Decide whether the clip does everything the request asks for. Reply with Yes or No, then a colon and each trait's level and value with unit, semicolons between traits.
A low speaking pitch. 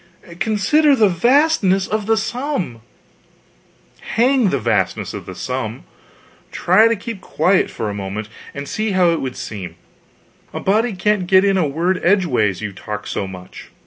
No: medium, 185 Hz